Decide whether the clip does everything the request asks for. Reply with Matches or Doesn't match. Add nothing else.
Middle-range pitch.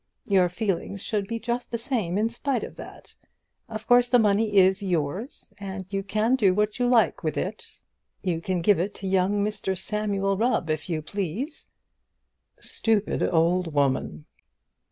Doesn't match